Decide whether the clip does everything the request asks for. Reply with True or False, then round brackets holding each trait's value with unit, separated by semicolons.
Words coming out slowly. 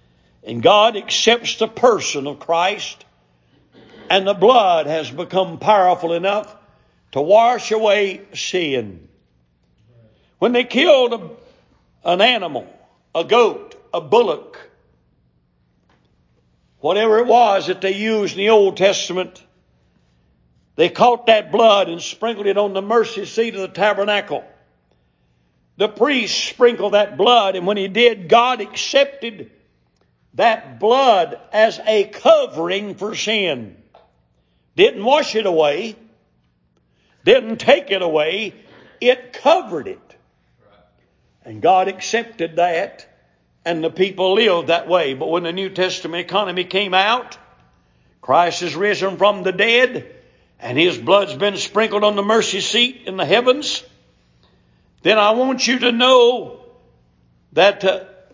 True (130 wpm)